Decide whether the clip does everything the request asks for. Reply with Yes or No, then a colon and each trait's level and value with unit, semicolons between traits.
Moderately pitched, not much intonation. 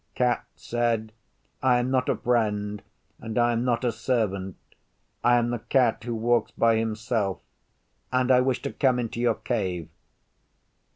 No: low, 120 Hz; narrow, 2.1 semitones